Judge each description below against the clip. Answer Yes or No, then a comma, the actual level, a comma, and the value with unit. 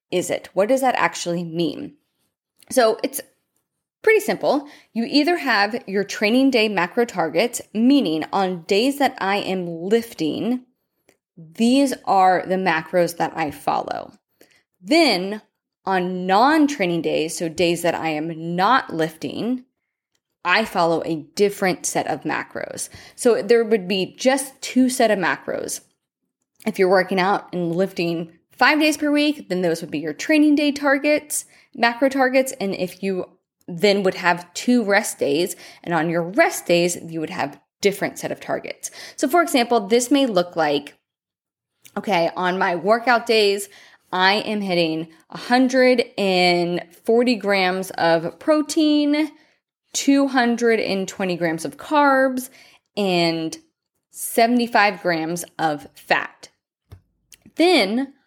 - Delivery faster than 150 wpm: No, slow, 135 wpm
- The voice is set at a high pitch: Yes, high, 200 Hz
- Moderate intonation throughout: No, wide, 6.8 semitones